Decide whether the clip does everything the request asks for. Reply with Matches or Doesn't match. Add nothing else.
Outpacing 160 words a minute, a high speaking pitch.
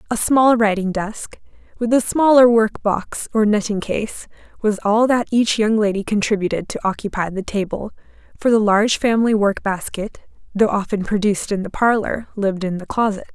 Matches